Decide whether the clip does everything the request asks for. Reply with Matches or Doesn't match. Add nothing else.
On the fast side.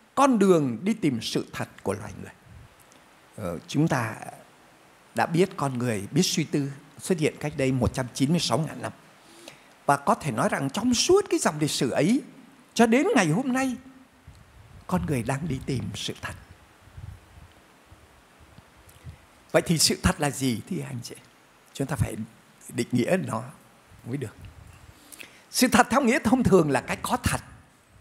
Doesn't match